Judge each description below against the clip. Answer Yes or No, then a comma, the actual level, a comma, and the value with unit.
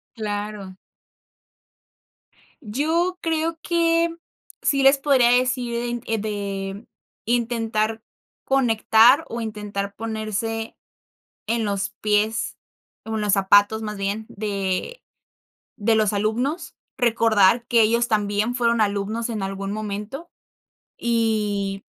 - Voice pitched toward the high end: Yes, high, 220 Hz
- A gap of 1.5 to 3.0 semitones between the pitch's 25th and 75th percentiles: Yes, average, 2.7 semitones